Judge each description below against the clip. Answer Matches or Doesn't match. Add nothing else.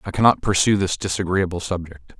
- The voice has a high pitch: Doesn't match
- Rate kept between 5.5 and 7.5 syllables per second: Matches